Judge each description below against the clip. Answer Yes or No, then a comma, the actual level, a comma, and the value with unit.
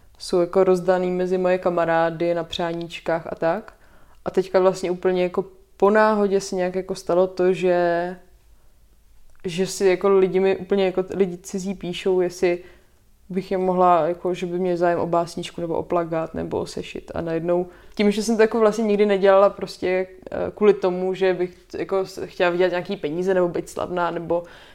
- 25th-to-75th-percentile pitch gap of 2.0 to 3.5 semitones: No, narrow, 1.6 semitones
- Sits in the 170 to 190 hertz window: Yes, medium, 185 Hz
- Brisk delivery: Yes, fast, 180 wpm